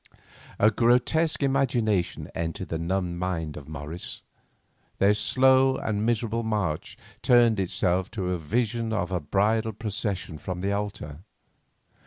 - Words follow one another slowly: Yes, slow, 130 wpm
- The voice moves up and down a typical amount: Yes, average, 4.6 semitones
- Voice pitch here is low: Yes, low, 100 Hz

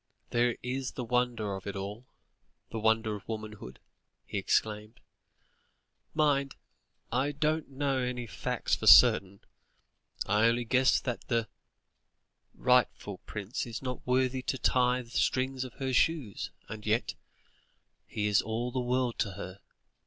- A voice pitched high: No, low, 120 Hz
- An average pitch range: Yes, average, 3.1 semitones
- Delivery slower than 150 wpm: Yes, average, 140 wpm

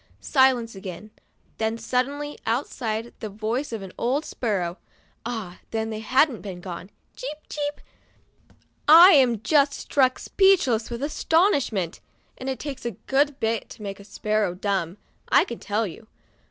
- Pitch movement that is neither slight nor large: Yes, average, 4.6 semitones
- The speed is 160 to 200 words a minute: No, average, 145 wpm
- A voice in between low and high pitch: No, high, 230 Hz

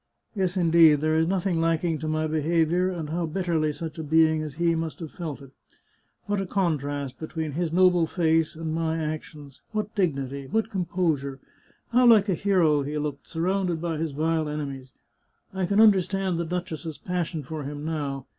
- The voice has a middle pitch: Yes, medium, 160 Hz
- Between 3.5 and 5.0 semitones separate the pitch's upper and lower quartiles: No, average, 2.8 semitones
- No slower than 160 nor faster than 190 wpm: Yes, average, 180 wpm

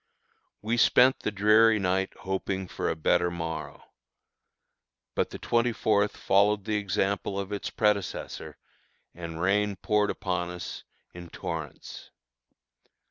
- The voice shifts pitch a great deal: No, average, 2.9 semitones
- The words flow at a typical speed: No, slow, 125 wpm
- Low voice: Yes, low, 100 Hz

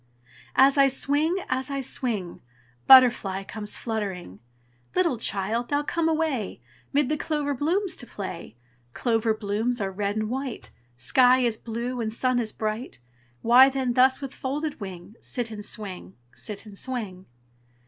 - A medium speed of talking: Yes, average, 150 wpm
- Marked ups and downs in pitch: No, average, 4.4 semitones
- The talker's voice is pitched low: No, high, 240 Hz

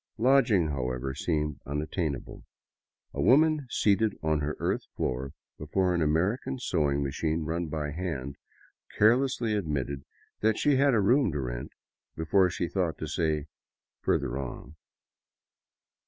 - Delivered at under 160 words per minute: Yes, average, 140 wpm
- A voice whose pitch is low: Yes, very low, 80 Hz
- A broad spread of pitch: Yes, wide, 6.8 semitones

